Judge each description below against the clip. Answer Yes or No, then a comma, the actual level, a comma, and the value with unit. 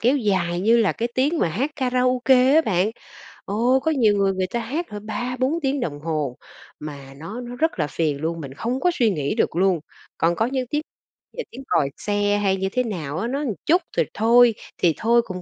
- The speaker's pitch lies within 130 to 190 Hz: No, high, 220 Hz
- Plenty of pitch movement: Yes, wide, 6.4 semitones